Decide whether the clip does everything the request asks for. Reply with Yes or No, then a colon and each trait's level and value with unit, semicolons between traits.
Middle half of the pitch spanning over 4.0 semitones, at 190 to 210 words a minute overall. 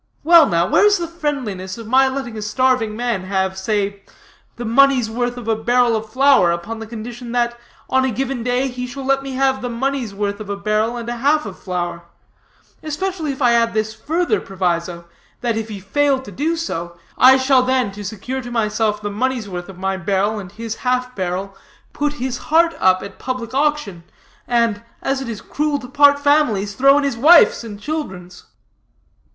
Yes: average, 4.8 semitones; average, 200 wpm